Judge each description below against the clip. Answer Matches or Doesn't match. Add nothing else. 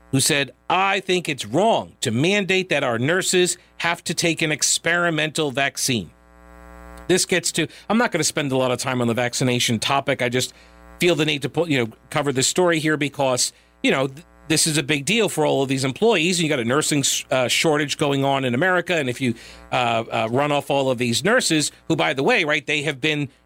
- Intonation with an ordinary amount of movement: Matches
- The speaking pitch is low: Doesn't match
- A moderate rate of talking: Doesn't match